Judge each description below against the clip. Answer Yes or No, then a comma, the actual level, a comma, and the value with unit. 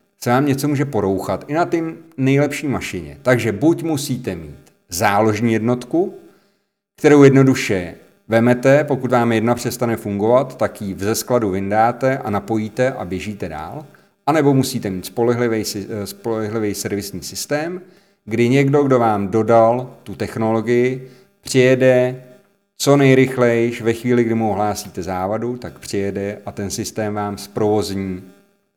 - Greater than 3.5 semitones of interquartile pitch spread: Yes, average, 4.3 semitones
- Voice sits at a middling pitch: No, low, 115 Hz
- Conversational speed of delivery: Yes, average, 135 wpm